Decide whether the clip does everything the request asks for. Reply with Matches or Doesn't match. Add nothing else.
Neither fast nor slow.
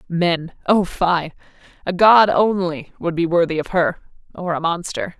Matches